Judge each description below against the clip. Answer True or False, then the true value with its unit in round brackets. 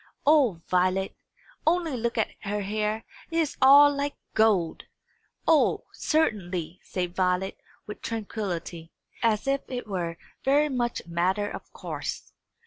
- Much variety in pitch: True (6.8 semitones)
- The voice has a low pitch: False (215 Hz)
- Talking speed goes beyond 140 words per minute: False (135 wpm)